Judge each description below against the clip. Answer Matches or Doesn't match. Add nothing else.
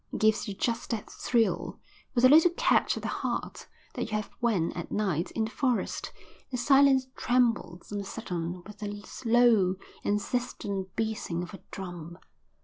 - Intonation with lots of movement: Doesn't match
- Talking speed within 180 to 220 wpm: Doesn't match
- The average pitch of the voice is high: Matches